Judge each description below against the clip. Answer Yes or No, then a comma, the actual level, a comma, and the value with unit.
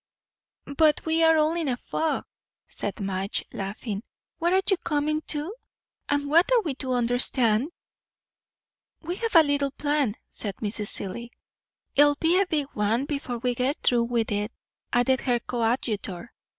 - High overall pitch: Yes, very high, 265 Hz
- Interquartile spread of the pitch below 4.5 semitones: No, average, 5.1 semitones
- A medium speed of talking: Yes, average, 155 wpm